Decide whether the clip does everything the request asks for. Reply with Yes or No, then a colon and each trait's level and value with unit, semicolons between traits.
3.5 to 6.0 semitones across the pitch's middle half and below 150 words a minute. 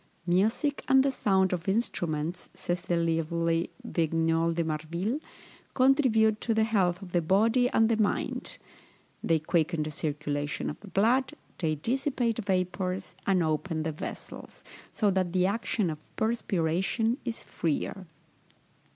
Yes: average, 5.2 semitones; average, 140 wpm